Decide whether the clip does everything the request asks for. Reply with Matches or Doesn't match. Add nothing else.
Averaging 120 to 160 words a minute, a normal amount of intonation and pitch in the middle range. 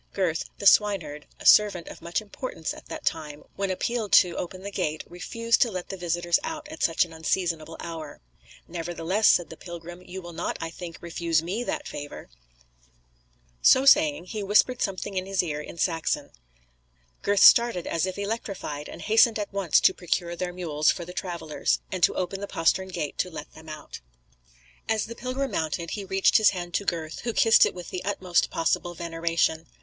Doesn't match